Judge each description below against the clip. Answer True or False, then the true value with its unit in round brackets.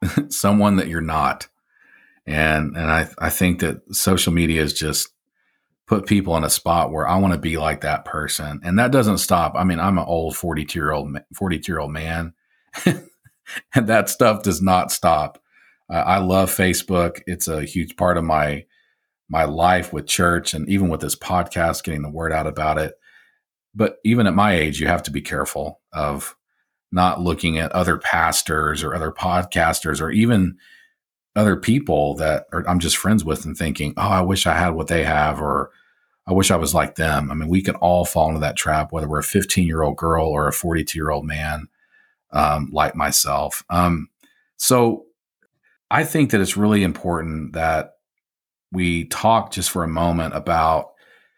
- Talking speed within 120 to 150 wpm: False (185 wpm)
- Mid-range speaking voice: False (85 Hz)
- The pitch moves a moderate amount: True (3.0 semitones)